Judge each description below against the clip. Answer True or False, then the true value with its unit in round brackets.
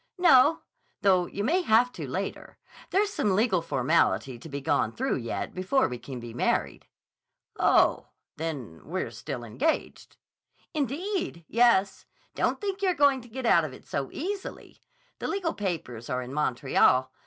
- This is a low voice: False (195 Hz)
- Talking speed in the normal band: True (155 wpm)